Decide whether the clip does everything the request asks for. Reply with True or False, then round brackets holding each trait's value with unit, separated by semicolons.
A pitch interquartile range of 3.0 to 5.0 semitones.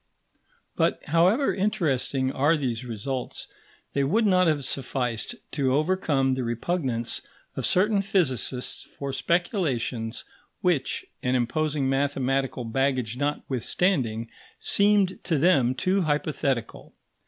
False (5.6 semitones)